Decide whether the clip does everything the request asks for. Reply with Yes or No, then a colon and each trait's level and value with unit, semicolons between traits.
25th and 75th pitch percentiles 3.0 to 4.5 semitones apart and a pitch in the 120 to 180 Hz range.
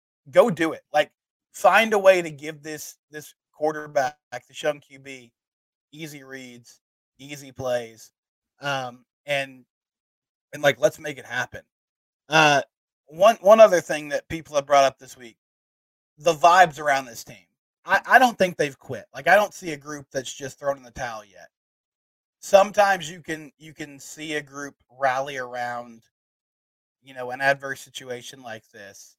Yes: average, 3.9 semitones; medium, 140 Hz